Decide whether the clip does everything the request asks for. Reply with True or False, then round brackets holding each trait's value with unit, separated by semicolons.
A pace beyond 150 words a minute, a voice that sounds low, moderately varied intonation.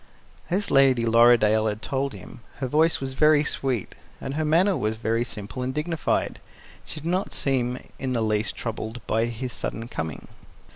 True (175 wpm; 125 Hz; 4.7 semitones)